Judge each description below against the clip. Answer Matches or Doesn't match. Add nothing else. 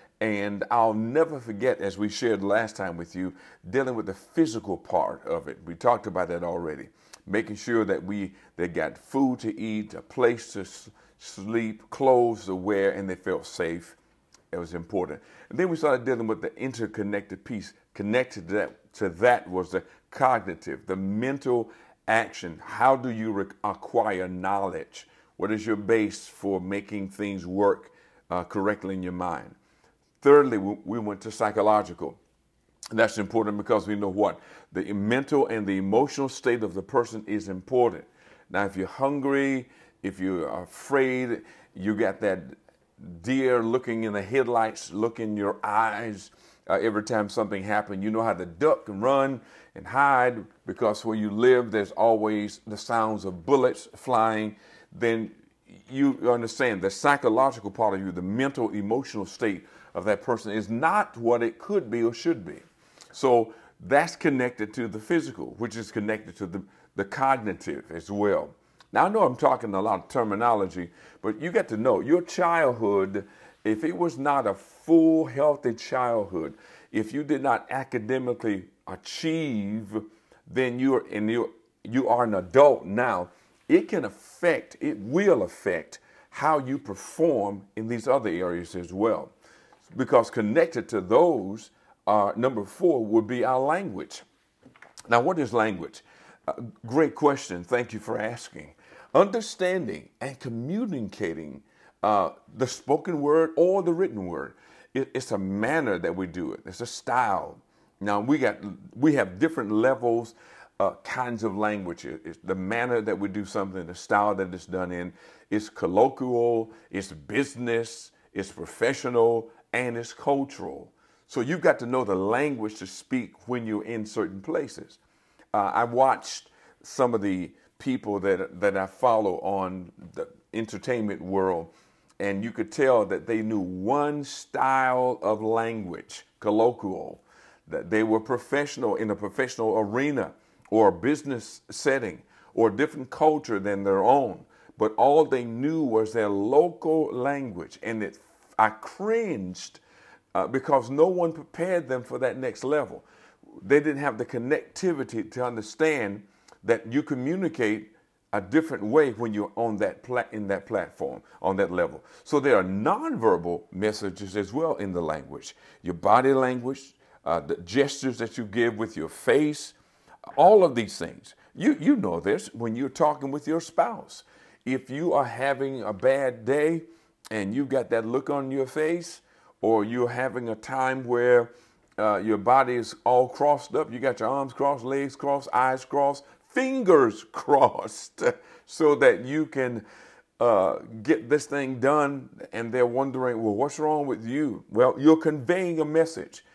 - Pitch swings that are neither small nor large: Matches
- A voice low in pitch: Matches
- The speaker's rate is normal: Matches